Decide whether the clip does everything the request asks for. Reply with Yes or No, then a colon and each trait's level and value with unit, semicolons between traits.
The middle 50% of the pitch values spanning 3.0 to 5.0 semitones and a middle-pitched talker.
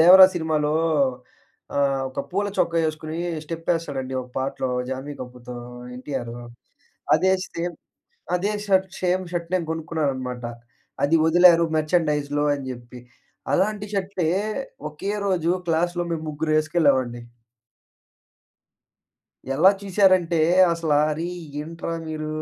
Yes: average, 3.7 semitones; medium, 160 Hz